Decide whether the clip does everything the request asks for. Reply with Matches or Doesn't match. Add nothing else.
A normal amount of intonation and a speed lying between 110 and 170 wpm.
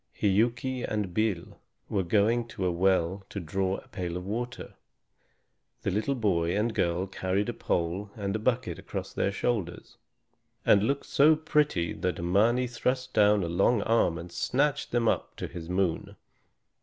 Matches